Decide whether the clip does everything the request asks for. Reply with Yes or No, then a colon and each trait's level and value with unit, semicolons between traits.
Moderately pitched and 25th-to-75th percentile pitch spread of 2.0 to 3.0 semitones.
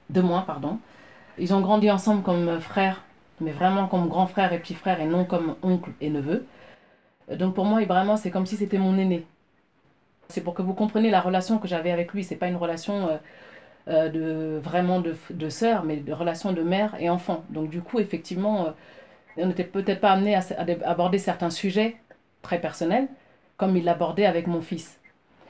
Yes: medium, 180 Hz; narrow, 2.5 semitones